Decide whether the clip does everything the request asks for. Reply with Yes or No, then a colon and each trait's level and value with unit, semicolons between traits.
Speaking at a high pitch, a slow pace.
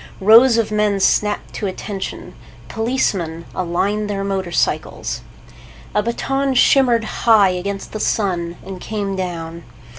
Yes: high, 200 Hz; slow, 120 wpm